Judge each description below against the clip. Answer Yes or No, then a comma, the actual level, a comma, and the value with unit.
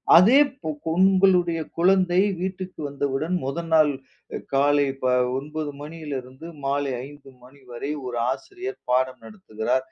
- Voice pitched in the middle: Yes, medium, 150 Hz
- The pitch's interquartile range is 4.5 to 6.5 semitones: Yes, average, 5.1 semitones